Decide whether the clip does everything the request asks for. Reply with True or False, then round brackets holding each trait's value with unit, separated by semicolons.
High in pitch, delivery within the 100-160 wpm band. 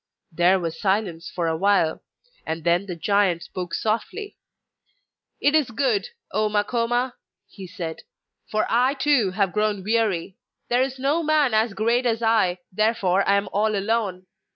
True (210 Hz; 155 wpm)